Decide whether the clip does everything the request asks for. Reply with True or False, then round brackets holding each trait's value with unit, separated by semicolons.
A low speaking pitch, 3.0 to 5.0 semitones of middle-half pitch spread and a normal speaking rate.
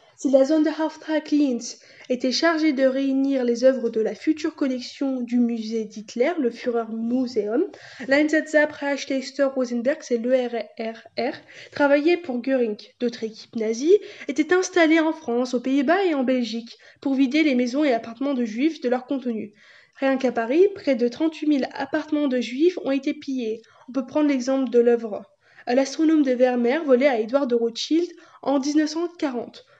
False (270 Hz; 3.9 semitones; 160 wpm)